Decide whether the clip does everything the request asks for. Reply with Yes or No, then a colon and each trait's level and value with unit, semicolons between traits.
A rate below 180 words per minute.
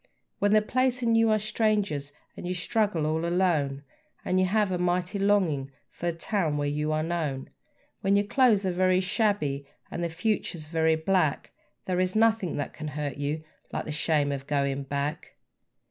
No: average, 185 wpm